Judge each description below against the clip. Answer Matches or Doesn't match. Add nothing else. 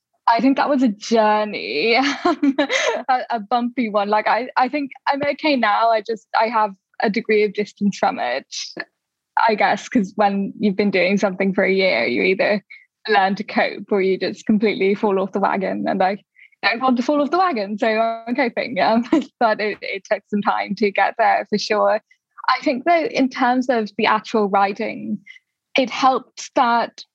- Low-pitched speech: Doesn't match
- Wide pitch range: Doesn't match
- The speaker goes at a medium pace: Matches